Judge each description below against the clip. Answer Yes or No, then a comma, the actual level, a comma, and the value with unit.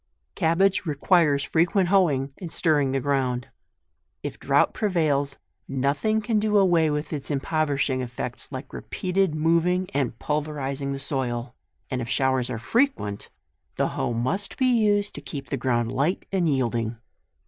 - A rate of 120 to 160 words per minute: Yes, average, 150 wpm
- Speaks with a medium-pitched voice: Yes, medium, 145 Hz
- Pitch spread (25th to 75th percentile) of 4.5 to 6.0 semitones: Yes, average, 5.3 semitones